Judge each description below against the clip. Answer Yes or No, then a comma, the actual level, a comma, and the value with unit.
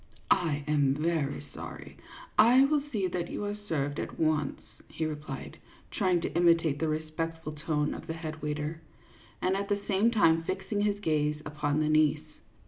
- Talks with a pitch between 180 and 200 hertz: No, medium, 160 Hz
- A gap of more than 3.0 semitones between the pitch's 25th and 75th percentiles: Yes, average, 3.8 semitones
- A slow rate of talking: No, average, 175 wpm